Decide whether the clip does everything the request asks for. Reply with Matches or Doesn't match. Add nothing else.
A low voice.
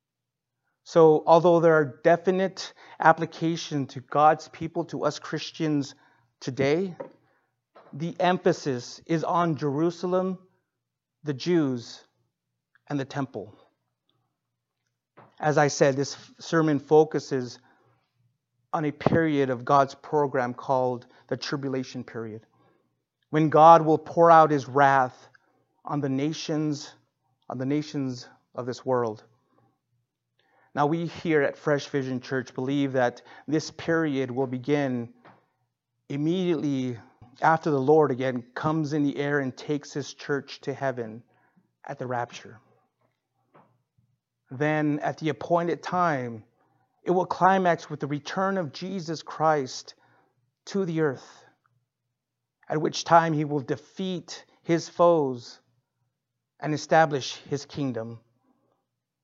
Doesn't match